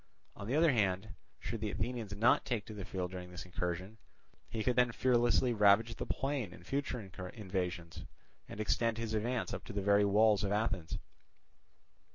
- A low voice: Yes, low, 105 Hz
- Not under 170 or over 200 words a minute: Yes, average, 175 wpm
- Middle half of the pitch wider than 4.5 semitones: No, average, 3.6 semitones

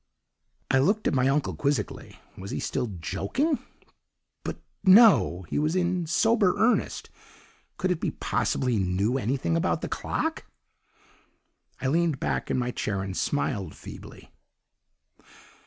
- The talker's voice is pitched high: No, low, 135 Hz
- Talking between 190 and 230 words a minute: No, average, 140 wpm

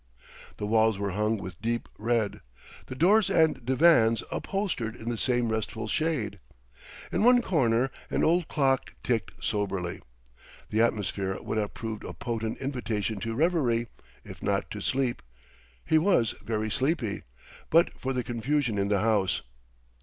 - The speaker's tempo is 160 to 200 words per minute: No, average, 150 wpm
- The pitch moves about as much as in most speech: Yes, average, 4.1 semitones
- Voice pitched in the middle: No, low, 115 Hz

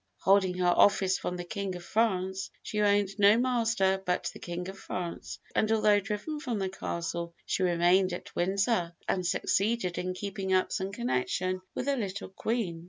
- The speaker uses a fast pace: No, average, 175 wpm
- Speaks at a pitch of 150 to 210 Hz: Yes, high, 190 Hz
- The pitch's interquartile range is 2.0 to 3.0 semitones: Yes, narrow, 2.5 semitones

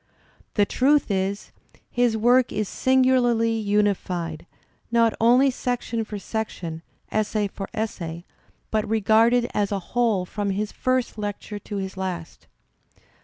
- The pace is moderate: No, slow, 125 wpm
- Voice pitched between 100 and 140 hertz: No, high, 215 Hz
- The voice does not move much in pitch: No, average, 3.2 semitones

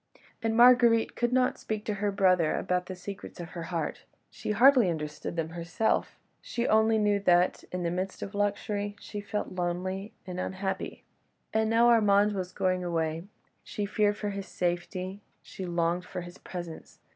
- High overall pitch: Yes, high, 195 Hz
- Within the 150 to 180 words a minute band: Yes, average, 170 wpm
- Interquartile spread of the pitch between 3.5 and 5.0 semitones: No, average, 3.0 semitones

